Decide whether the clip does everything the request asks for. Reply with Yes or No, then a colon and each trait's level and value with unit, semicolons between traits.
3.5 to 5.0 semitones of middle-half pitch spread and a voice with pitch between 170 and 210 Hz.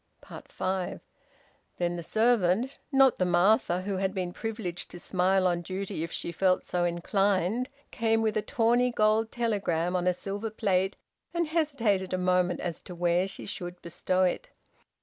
Yes: average, 3.8 semitones; high, 190 Hz